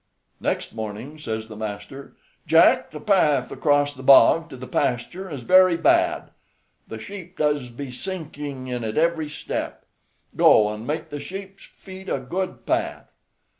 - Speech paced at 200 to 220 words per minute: No, average, 155 wpm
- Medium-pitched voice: Yes, medium, 145 Hz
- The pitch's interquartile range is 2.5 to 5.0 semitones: No, wide, 5.5 semitones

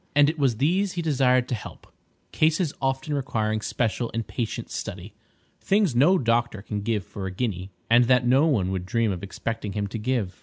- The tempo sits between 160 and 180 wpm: No, average, 190 wpm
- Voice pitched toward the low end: Yes, low, 120 Hz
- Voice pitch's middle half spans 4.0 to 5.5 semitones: Yes, average, 4.6 semitones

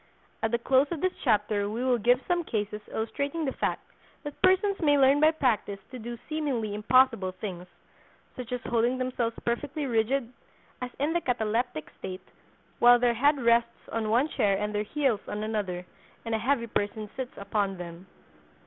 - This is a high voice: Yes, high, 235 Hz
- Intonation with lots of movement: No, average, 4.4 semitones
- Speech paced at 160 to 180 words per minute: Yes, average, 175 wpm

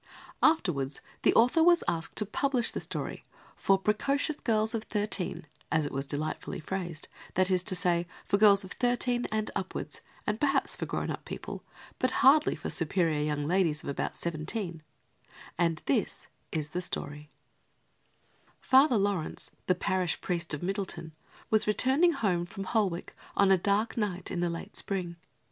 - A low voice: No, high, 190 Hz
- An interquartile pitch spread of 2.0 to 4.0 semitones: No, average, 4.5 semitones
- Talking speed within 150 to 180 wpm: Yes, average, 160 wpm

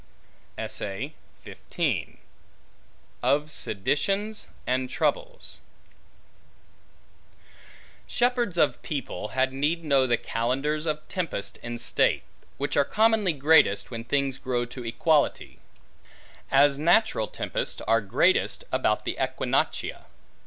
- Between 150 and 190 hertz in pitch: No, medium, 140 Hz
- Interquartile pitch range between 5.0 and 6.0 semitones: Yes, wide, 5.5 semitones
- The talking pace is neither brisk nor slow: No, slow, 95 wpm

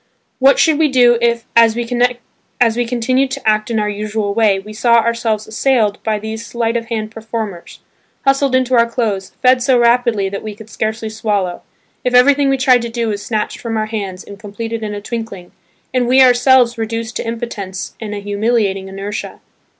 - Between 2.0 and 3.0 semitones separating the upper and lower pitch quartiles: Yes, narrow, 2.5 semitones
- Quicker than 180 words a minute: Yes, average, 190 wpm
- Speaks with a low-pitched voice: No, high, 230 Hz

